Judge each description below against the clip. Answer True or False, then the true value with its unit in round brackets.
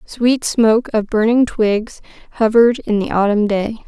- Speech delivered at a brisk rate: False (155 wpm)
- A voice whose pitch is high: True (225 Hz)